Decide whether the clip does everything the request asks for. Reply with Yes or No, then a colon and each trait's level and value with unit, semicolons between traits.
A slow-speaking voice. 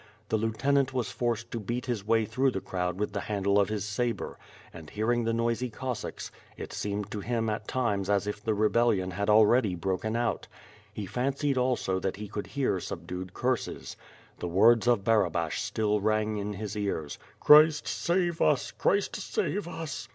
No: average, 180 wpm